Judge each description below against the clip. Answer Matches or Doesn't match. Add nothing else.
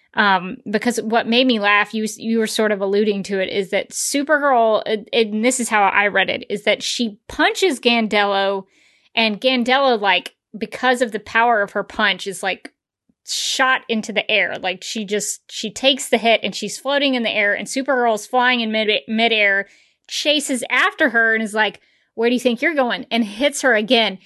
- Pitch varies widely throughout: Doesn't match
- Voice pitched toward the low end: Doesn't match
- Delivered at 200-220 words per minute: Matches